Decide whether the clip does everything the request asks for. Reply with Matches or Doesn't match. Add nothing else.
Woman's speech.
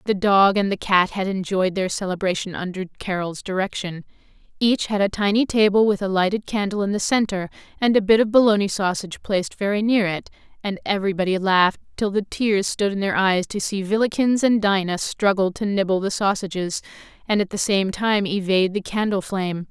Matches